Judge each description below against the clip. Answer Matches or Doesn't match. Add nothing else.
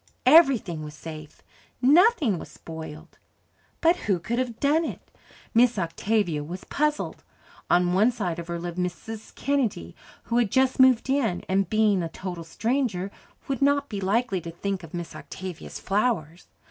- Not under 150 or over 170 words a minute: Matches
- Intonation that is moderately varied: Doesn't match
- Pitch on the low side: Doesn't match